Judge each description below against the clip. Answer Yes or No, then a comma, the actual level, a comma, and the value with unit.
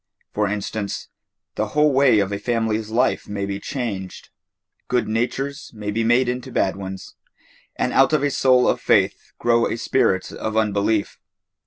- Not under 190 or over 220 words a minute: No, average, 165 wpm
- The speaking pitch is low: Yes, low, 110 Hz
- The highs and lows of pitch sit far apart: No, average, 3.6 semitones